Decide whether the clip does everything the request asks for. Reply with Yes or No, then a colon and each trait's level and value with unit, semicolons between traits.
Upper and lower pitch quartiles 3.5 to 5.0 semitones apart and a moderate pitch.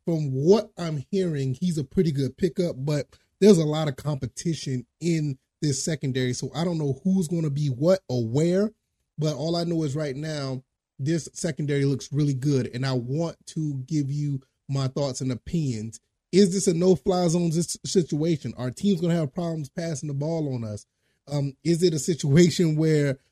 Yes: average, 4.0 semitones; medium, 155 Hz